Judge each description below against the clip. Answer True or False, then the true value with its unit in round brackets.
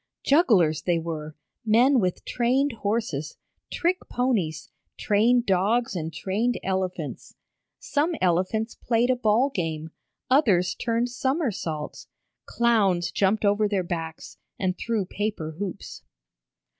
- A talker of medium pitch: False (205 Hz)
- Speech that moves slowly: True (115 wpm)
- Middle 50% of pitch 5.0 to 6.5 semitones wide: True (5.5 semitones)